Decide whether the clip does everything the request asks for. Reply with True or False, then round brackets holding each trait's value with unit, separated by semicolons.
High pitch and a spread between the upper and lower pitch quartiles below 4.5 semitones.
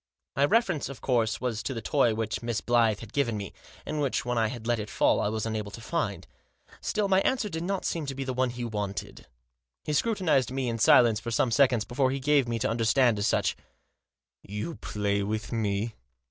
False (120 Hz; 3.9 semitones)